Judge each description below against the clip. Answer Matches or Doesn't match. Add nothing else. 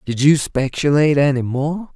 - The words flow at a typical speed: Matches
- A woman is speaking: Doesn't match